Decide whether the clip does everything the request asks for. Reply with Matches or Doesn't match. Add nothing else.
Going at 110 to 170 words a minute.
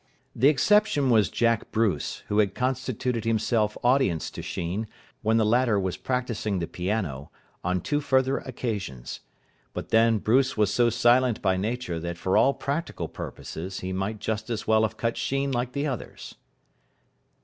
Matches